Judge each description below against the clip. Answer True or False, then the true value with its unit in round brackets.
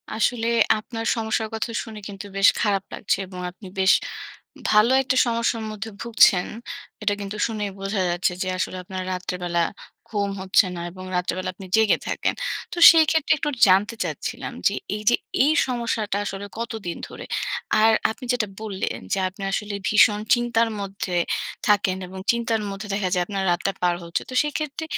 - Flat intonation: False (3.2 semitones)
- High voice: True (210 Hz)